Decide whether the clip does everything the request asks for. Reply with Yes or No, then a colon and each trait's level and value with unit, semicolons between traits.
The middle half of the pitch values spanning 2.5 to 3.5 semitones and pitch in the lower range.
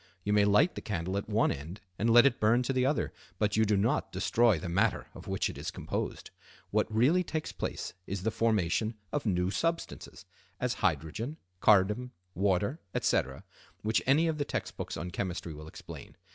No: average, 5.1 semitones; low, 105 Hz